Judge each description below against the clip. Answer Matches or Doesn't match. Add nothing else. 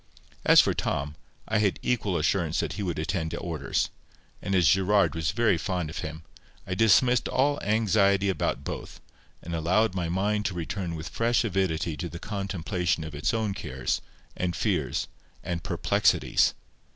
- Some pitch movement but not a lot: Matches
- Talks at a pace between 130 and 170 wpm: Matches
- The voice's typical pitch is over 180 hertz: Doesn't match